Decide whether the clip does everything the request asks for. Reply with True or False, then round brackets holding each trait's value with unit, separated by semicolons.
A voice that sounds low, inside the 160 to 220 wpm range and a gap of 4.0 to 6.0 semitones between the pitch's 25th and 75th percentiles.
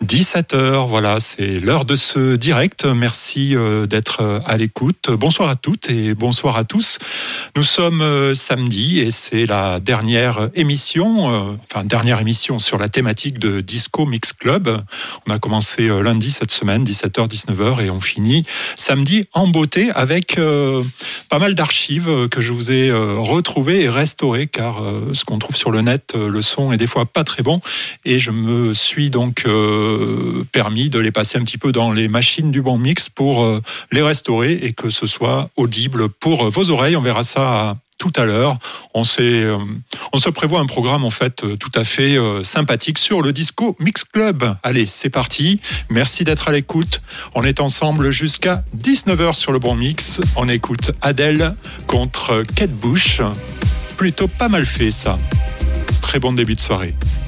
True (125 Hz; 180 wpm; 5.1 semitones)